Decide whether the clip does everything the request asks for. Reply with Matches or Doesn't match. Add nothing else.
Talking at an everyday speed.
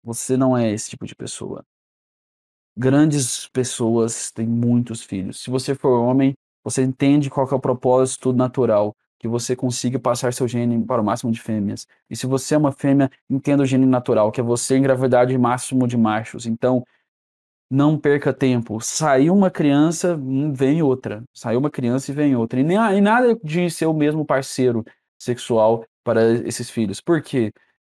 Matches